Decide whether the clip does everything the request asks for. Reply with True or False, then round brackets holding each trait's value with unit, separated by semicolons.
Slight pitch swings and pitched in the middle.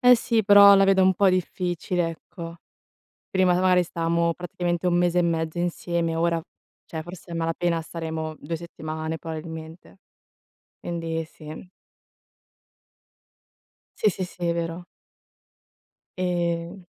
True (1.7 semitones; 170 Hz)